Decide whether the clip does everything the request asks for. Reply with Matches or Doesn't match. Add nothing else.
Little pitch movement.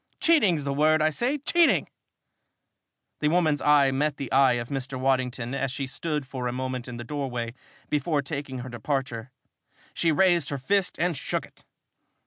Doesn't match